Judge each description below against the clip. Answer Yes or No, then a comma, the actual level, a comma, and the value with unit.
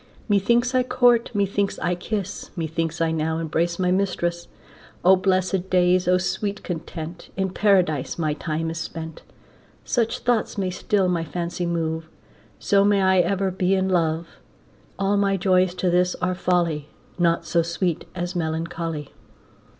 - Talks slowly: No, average, 150 wpm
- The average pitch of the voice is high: No, medium, 180 Hz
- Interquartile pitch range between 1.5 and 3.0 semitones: Yes, average, 2.7 semitones